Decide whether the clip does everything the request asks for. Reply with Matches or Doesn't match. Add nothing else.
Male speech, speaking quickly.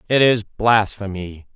Doesn't match